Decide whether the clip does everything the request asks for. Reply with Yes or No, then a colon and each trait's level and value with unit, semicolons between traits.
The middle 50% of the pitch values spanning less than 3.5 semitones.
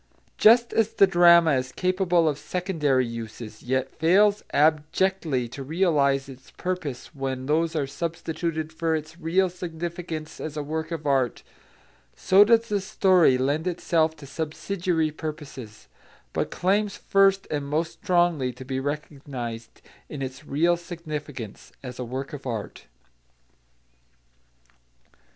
No: average, 4.3 semitones